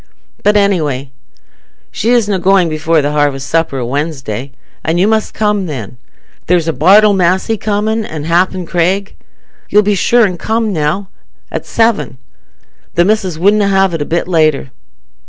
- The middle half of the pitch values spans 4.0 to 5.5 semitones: Yes, average, 4.9 semitones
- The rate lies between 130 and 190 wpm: Yes, average, 155 wpm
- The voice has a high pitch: No, medium, 180 Hz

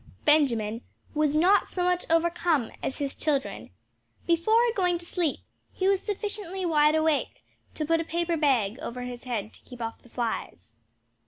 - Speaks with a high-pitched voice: Yes, very high, 310 Hz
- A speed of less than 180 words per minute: Yes, average, 165 wpm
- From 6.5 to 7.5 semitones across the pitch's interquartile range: No, wide, 5.8 semitones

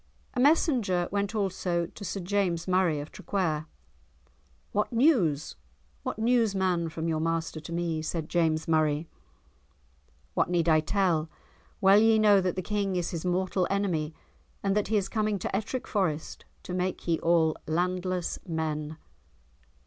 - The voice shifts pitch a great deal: No, average, 3.7 semitones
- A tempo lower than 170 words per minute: Yes, average, 155 wpm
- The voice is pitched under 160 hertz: No, medium, 180 Hz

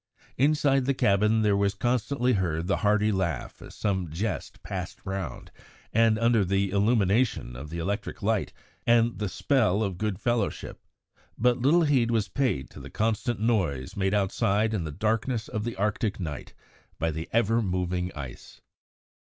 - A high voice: No, low, 105 Hz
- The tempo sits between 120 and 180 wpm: Yes, average, 160 wpm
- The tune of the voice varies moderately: Yes, average, 3.6 semitones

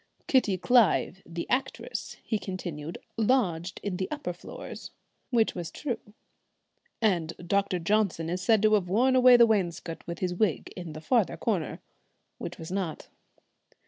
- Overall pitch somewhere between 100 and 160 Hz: No, high, 190 Hz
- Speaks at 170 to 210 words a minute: No, average, 150 wpm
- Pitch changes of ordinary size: Yes, average, 4.7 semitones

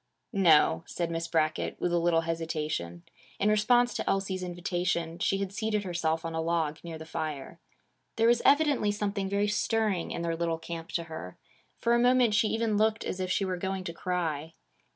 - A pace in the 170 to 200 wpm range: Yes, average, 195 wpm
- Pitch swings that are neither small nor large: Yes, average, 4.1 semitones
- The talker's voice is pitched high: No, medium, 175 Hz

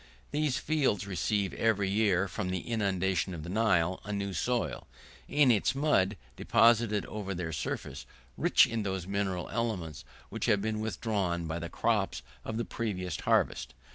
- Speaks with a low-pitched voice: Yes, low, 100 Hz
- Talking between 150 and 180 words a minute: Yes, average, 160 wpm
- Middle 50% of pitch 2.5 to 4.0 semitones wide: Yes, average, 3.4 semitones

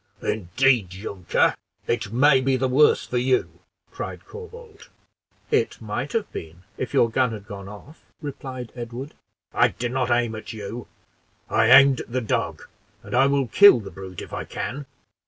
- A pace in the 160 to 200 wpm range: Yes, average, 170 wpm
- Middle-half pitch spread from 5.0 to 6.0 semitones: No, average, 3.9 semitones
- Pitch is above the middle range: No, low, 125 Hz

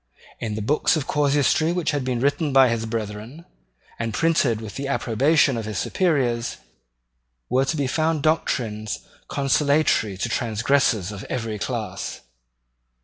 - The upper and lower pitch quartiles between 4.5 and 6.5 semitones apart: Yes, average, 4.8 semitones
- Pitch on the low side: Yes, low, 125 Hz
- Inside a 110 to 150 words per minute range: Yes, average, 145 wpm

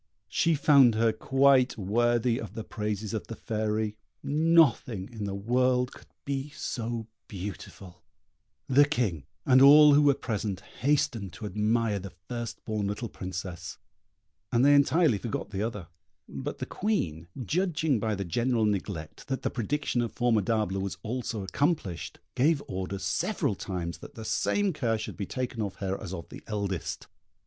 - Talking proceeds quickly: No, average, 160 wpm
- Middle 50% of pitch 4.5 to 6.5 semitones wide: Yes, average, 4.8 semitones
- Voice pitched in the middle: No, low, 110 Hz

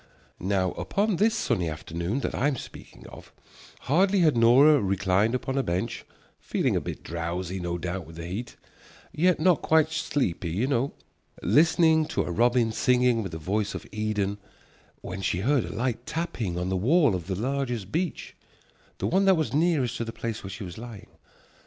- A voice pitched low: Yes, low, 115 Hz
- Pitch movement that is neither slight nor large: No, wide, 7.7 semitones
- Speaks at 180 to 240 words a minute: Yes, average, 185 wpm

